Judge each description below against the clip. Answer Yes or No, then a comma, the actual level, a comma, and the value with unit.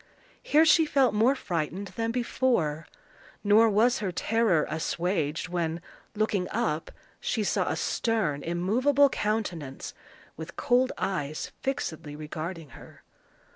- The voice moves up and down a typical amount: No, wide, 6.5 semitones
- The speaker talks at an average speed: No, slow, 120 wpm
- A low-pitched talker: No, high, 200 Hz